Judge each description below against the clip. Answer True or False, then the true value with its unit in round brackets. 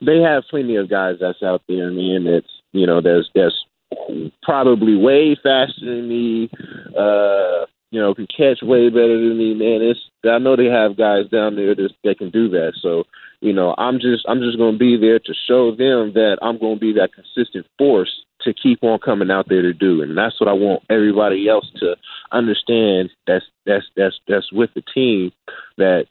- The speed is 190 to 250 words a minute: True (200 wpm)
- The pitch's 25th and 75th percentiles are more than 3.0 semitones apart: True (3.5 semitones)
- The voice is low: True (115 Hz)